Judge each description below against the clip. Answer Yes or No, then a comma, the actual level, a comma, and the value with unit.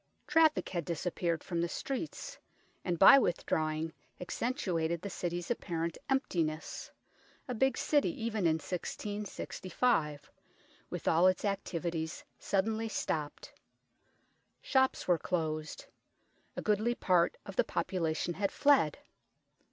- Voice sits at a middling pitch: Yes, medium, 180 Hz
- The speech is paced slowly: Yes, slow, 115 wpm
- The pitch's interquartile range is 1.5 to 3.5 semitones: No, average, 5.3 semitones